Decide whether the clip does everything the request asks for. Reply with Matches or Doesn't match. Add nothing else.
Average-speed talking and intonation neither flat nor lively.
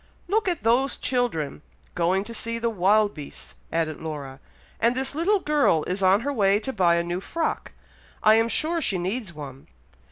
Doesn't match